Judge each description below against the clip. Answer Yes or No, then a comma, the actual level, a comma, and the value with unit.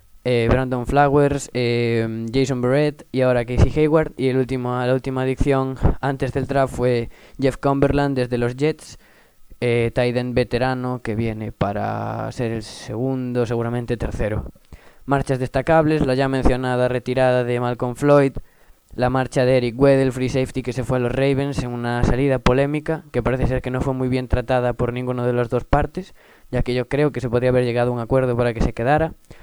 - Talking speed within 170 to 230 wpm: Yes, fast, 190 wpm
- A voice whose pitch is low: Yes, low, 125 Hz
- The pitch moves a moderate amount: No, narrow, 1.8 semitones